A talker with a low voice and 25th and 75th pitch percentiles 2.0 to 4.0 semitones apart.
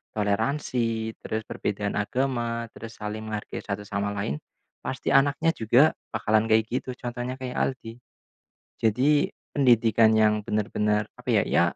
Yes: low, 110 Hz; average, 2.9 semitones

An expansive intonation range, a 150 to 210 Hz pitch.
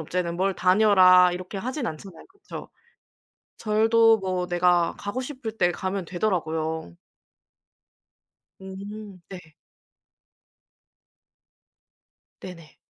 No: average, 3.4 semitones; high, 190 Hz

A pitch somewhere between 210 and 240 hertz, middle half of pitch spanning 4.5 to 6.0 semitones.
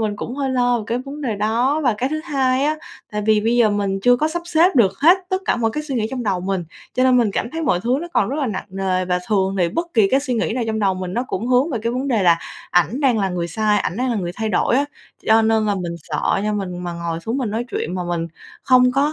Yes: high, 225 Hz; average, 5.1 semitones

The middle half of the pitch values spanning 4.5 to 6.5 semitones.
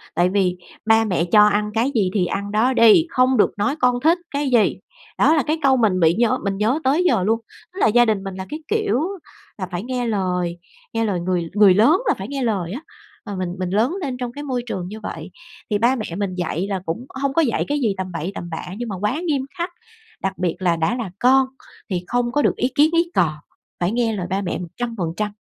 Yes: wide, 5.5 semitones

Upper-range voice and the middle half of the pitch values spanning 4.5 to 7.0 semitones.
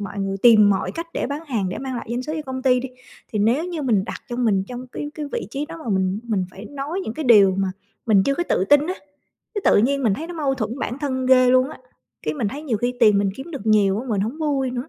Yes: very high, 250 Hz; average, 5.1 semitones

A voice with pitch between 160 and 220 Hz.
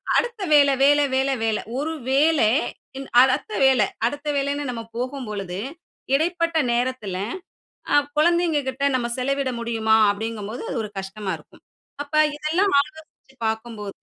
No: very high, 265 Hz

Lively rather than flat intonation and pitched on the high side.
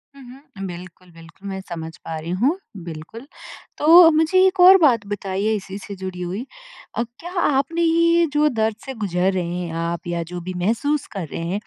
Yes: wide, 8.8 semitones; high, 200 Hz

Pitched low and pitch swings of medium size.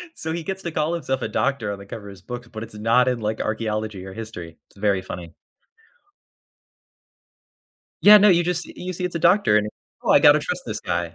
No: low, 115 Hz; wide, 8.6 semitones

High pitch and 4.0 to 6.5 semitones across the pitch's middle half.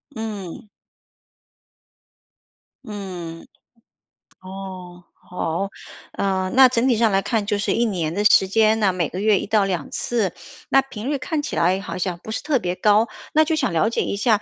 No: high, 205 Hz; average, 3.5 semitones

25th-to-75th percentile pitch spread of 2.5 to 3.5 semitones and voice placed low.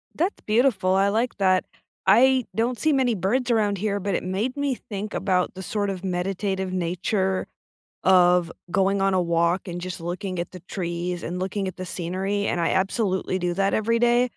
No: average, 2.8 semitones; high, 190 Hz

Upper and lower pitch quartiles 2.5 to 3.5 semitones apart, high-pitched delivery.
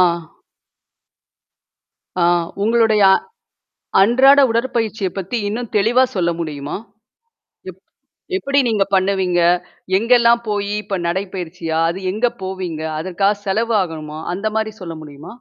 No: average, 4.2 semitones; high, 195 Hz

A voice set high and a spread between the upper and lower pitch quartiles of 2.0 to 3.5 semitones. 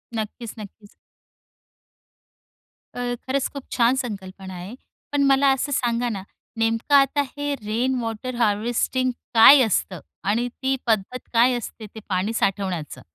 No: high, 230 Hz; average, 3.9 semitones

